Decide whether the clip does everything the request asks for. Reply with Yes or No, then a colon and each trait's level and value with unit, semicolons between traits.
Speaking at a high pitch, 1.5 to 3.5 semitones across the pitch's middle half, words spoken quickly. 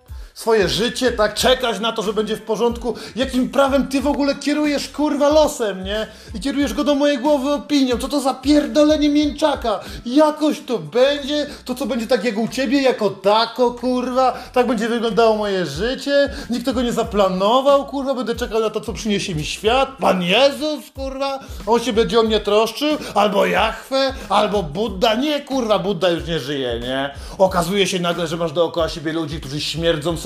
No: high, 235 Hz; average, 5.1 semitones; fast, 185 wpm